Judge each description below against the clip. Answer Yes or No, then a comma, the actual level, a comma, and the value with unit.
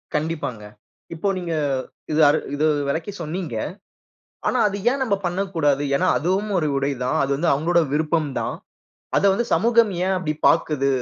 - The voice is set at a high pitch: No, medium, 165 Hz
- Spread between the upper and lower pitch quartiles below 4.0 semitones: No, average, 4.3 semitones